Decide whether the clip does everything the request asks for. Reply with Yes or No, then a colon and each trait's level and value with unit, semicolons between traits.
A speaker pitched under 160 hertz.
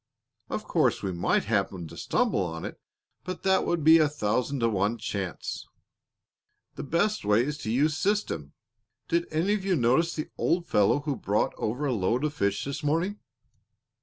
Yes: medium, 140 Hz